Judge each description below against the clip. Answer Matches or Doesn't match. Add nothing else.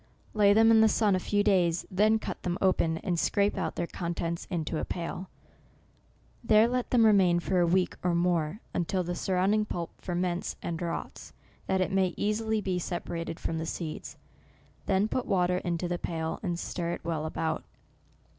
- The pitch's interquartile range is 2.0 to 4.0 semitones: Matches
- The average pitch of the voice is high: Doesn't match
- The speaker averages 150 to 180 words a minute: Doesn't match